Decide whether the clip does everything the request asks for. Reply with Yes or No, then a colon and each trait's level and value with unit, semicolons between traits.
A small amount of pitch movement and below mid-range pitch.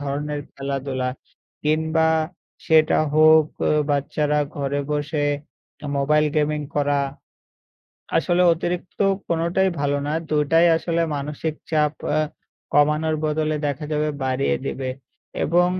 No: narrow, 1.7 semitones; medium, 150 Hz